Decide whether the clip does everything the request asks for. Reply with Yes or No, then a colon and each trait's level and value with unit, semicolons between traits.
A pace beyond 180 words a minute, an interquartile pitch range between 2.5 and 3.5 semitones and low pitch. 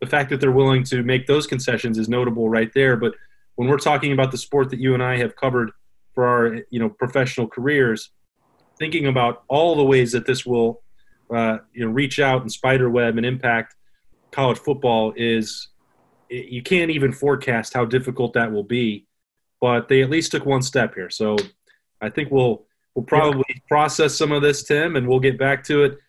Yes: average, 200 wpm; average, 2.8 semitones; low, 130 Hz